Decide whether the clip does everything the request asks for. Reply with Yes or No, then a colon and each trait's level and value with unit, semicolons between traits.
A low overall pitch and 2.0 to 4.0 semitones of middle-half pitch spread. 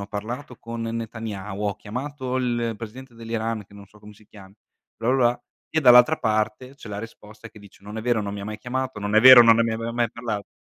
Yes: low, 115 Hz; narrow, 2.6 semitones